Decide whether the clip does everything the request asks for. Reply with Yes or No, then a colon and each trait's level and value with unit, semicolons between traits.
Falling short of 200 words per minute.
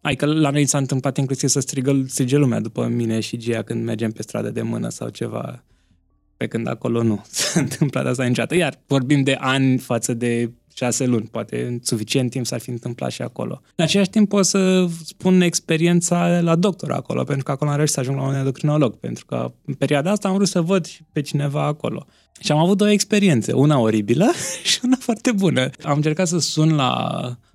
No: fast, 205 wpm